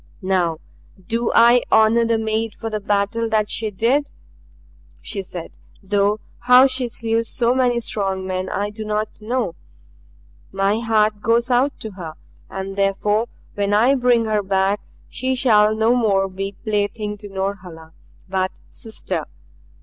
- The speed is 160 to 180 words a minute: No, average, 150 wpm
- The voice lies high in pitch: Yes, high, 215 Hz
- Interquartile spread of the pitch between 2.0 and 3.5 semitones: Yes, average, 2.8 semitones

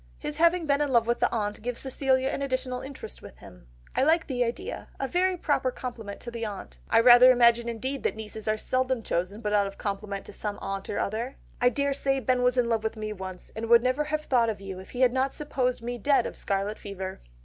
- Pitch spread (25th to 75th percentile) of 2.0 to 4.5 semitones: Yes, average, 3.9 semitones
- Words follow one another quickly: Yes, fast, 240 wpm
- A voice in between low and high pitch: No, high, 240 Hz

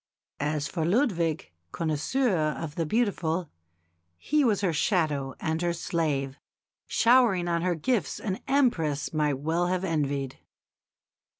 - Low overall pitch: No, medium, 165 Hz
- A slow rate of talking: Yes, slow, 125 wpm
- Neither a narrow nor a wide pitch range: Yes, average, 4.1 semitones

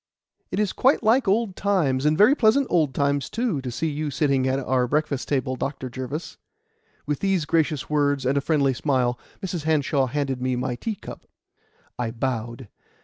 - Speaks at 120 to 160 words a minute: No, average, 180 wpm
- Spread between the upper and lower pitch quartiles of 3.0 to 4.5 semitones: Yes, average, 4.2 semitones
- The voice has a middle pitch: Yes, medium, 145 Hz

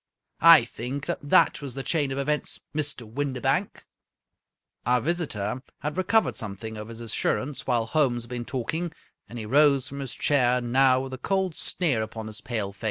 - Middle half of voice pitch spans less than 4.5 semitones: Yes, average, 3.9 semitones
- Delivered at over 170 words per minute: Yes, average, 185 wpm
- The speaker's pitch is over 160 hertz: No, low, 130 Hz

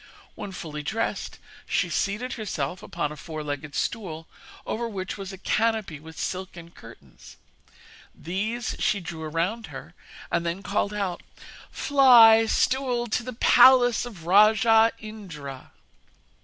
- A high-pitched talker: Yes, high, 200 Hz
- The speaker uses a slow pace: Yes, slow, 130 wpm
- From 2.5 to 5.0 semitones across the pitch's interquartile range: No, wide, 5.5 semitones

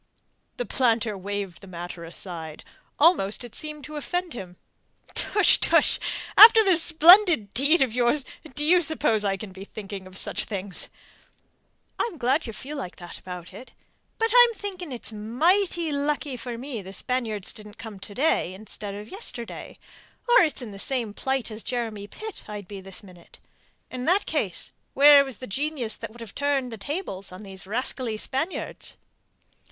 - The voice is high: Yes, high, 240 Hz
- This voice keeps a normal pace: Yes, average, 175 wpm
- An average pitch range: No, wide, 6.9 semitones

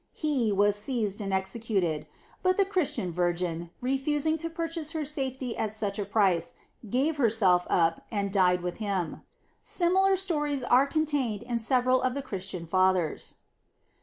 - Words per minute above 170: No, average, 150 wpm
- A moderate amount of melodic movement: No, wide, 7.4 semitones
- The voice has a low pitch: No, high, 230 Hz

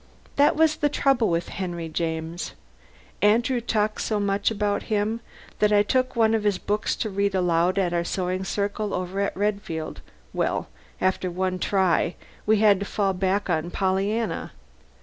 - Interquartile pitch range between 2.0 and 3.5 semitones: Yes, average, 2.8 semitones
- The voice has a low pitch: No, high, 200 Hz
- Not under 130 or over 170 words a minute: Yes, average, 165 wpm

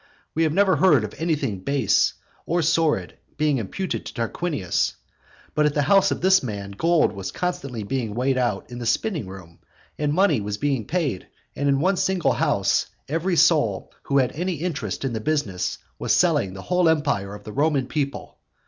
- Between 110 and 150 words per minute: No, average, 185 wpm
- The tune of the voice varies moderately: No, wide, 7.3 semitones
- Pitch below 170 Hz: Yes, medium, 140 Hz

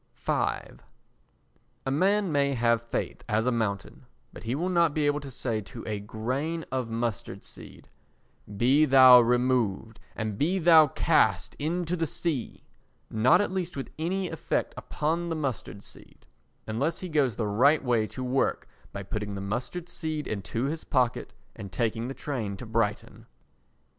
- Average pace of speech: Yes, average, 160 wpm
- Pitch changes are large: Yes, wide, 5.8 semitones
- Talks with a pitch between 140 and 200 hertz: No, low, 130 Hz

